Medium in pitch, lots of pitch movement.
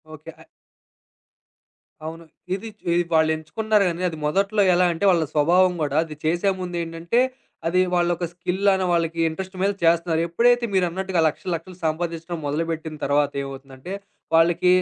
No: medium, 170 Hz; average, 2.7 semitones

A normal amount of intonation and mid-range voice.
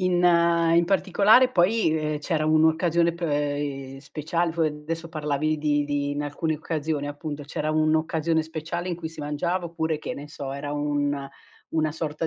No: narrow, 2.3 semitones; medium, 155 Hz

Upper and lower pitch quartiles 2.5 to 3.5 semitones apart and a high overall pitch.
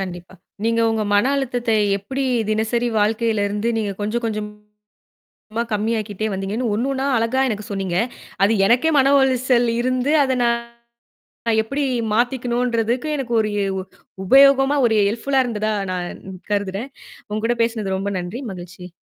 Yes: average, 3.2 semitones; high, 225 Hz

